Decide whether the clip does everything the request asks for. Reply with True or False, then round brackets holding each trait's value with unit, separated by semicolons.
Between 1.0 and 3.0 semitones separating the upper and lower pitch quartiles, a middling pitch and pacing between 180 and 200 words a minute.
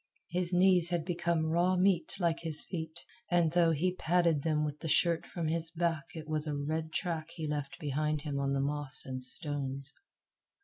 True (2.6 semitones; 160 Hz; 190 wpm)